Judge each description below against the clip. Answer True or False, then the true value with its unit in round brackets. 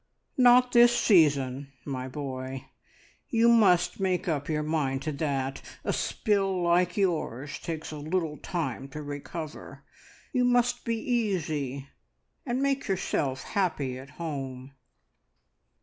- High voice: False (160 Hz)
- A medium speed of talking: False (125 wpm)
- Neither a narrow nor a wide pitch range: False (6.3 semitones)